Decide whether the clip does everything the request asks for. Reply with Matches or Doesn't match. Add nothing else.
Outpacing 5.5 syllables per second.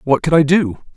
Doesn't match